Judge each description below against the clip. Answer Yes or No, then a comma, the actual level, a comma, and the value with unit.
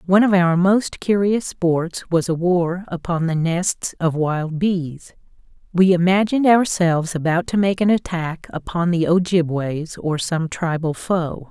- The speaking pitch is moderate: Yes, medium, 175 Hz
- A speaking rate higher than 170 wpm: No, average, 155 wpm